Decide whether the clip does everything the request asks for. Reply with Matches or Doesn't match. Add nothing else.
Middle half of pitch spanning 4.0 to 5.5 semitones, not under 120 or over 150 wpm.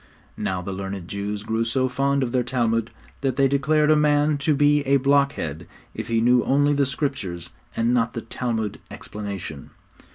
Doesn't match